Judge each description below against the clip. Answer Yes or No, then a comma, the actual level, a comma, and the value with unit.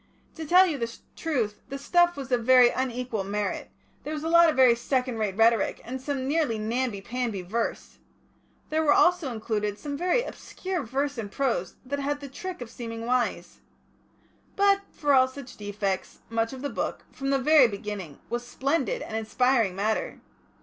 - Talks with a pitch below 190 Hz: No, very high, 255 Hz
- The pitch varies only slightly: No, average, 4.4 semitones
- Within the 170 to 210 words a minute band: Yes, average, 180 wpm